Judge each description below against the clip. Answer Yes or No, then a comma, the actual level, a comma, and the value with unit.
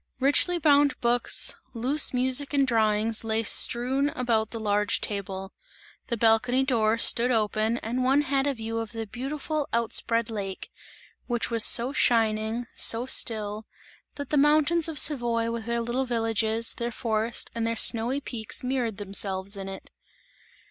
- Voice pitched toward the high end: Yes, high, 230 Hz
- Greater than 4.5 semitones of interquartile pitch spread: No, average, 3.1 semitones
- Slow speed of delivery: No, average, 155 wpm